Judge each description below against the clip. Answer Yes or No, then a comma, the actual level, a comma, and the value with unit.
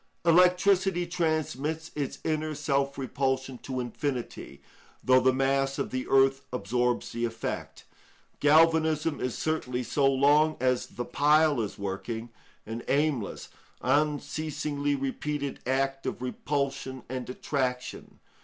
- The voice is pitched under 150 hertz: Yes, low, 135 Hz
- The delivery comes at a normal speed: No, slow, 115 wpm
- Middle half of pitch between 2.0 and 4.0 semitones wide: Yes, average, 3.1 semitones